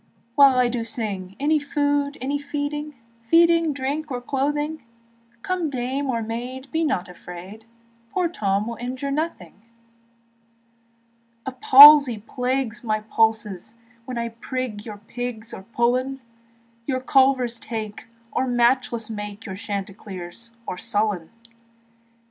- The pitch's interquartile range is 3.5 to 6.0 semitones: Yes, average, 4.4 semitones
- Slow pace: Yes, slow, 125 wpm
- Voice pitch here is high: Yes, high, 245 Hz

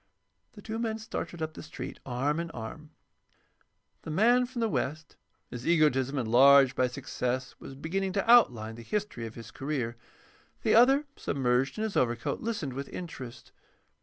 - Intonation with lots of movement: Yes, wide, 8.3 semitones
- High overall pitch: No, medium, 145 Hz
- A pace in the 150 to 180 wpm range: Yes, average, 165 wpm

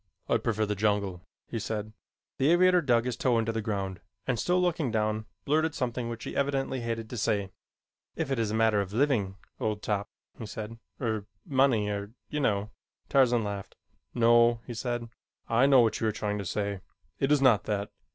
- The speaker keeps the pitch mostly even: No, average, 3.6 semitones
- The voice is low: Yes, low, 115 Hz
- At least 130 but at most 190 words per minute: No, average, 200 wpm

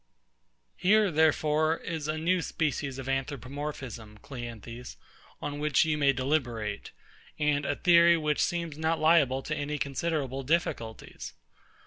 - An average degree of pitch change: Yes, average, 3.2 semitones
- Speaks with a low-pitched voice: No, medium, 150 Hz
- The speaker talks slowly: Yes, slow, 125 wpm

